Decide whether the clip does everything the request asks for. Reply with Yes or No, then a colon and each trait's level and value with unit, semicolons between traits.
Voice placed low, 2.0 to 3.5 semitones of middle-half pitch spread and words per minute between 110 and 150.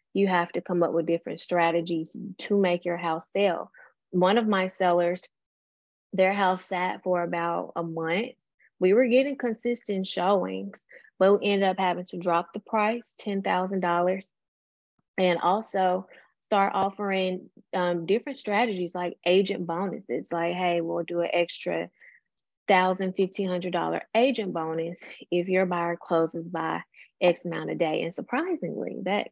No: medium, 180 Hz; narrow, 2.5 semitones; average, 145 wpm